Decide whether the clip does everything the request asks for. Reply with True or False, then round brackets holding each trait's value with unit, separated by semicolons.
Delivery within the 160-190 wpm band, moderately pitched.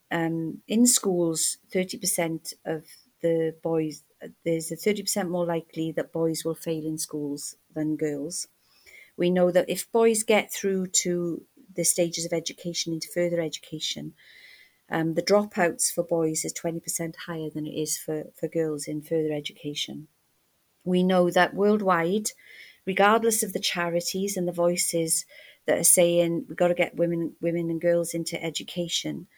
True (165 wpm; 170 Hz)